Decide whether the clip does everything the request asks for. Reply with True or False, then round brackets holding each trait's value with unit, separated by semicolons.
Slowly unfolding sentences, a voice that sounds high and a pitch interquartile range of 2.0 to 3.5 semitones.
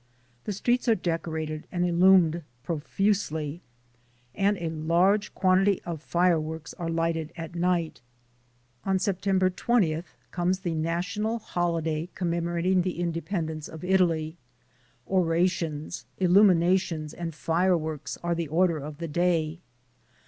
False (115 wpm; 170 Hz; 2.4 semitones)